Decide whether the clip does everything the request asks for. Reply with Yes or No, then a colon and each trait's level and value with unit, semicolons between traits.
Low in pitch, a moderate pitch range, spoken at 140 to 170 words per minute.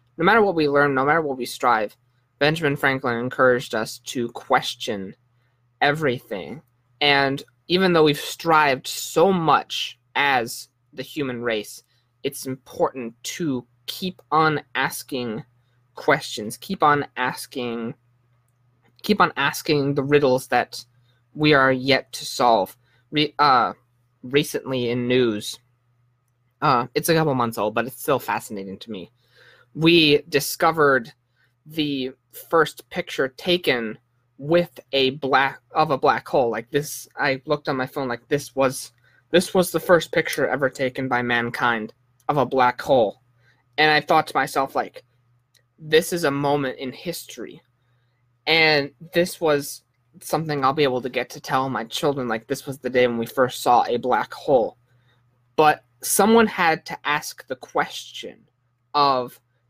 Yes: low, 130 Hz; average, 3.1 semitones; average, 150 wpm